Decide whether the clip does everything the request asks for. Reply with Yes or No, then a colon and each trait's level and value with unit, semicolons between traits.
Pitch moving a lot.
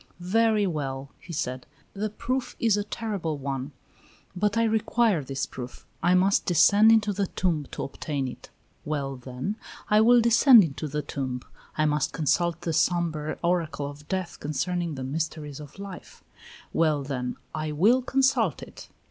Yes: wide, 6.3 semitones